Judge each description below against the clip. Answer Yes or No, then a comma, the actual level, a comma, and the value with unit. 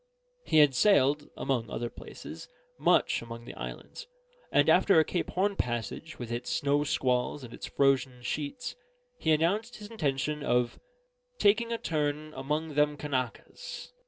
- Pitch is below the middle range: No, medium, 145 Hz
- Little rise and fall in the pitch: No, average, 4.3 semitones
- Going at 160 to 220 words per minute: No, average, 150 wpm